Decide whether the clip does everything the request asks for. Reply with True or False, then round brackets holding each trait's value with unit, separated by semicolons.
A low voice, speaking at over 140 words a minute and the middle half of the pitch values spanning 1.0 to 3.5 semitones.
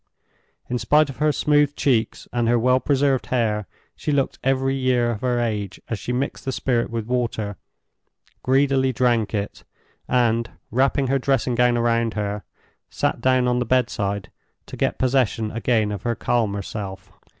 True (120 Hz; 165 wpm; 2.8 semitones)